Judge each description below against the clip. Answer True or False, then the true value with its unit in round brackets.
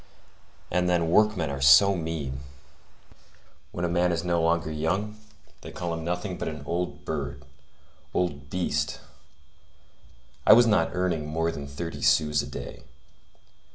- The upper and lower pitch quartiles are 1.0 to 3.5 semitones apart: True (2.7 semitones)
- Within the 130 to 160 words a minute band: True (145 wpm)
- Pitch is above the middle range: False (85 Hz)